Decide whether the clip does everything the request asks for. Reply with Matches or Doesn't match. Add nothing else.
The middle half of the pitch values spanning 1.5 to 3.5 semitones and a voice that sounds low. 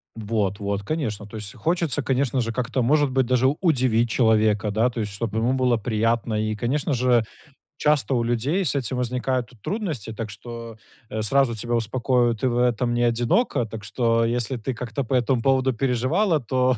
Matches